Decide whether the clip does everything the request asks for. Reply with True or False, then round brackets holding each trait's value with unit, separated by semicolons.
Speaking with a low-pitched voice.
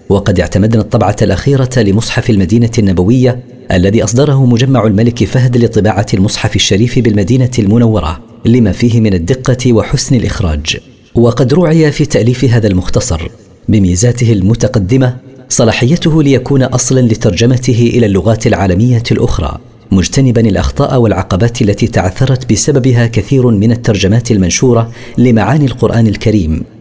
True (115 Hz)